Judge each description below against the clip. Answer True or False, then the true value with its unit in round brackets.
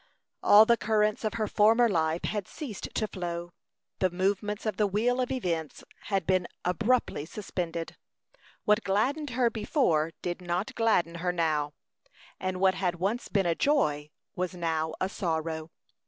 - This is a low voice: False (190 Hz)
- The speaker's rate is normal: True (155 wpm)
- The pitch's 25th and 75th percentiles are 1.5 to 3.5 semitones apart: False (4.2 semitones)